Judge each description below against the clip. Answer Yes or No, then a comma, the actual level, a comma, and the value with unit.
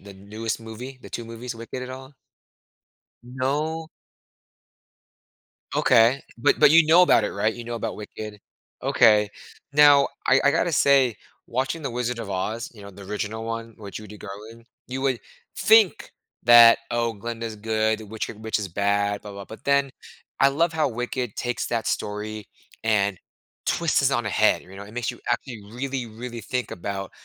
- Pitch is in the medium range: No, low, 115 Hz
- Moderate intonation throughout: Yes, average, 3.4 semitones